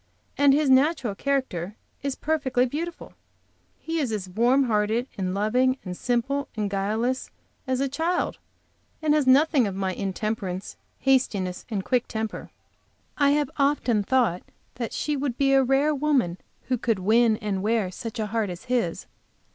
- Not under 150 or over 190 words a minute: Yes, average, 160 wpm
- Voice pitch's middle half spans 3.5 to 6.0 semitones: Yes, average, 4.9 semitones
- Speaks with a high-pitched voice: Yes, high, 245 Hz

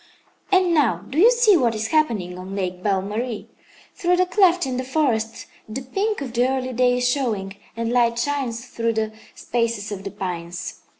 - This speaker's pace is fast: No, average, 190 wpm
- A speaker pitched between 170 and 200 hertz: No, high, 240 Hz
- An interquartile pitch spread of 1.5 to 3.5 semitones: No, wide, 5.5 semitones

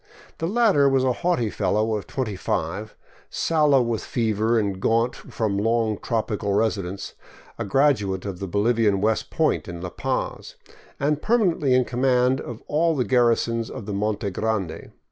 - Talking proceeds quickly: No, average, 160 wpm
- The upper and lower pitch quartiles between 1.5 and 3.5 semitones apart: No, average, 4.3 semitones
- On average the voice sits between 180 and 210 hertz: No, low, 115 Hz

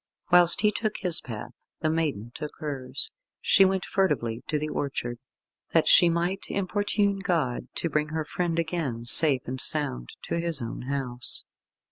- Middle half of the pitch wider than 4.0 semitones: Yes, wide, 5.5 semitones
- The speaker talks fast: No, average, 160 wpm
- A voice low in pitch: No, medium, 155 Hz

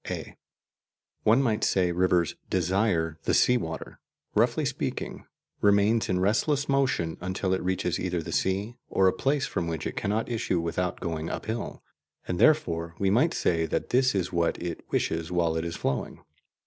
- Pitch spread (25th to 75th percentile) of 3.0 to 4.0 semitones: No, average, 4.7 semitones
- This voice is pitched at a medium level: No, very low, 95 Hz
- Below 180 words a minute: Yes, average, 170 wpm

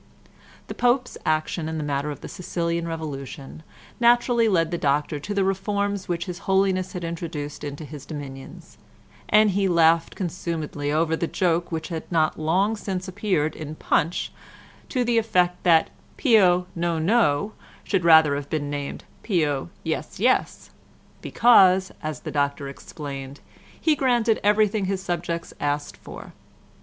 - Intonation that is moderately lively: Yes, average, 4.3 semitones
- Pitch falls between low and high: Yes, medium, 170 Hz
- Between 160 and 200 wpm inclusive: No, average, 150 wpm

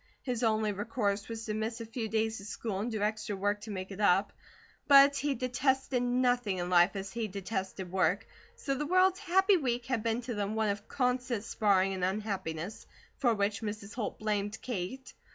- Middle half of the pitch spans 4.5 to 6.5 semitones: No, average, 3.6 semitones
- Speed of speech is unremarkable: Yes, average, 195 wpm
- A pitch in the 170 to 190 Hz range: No, high, 220 Hz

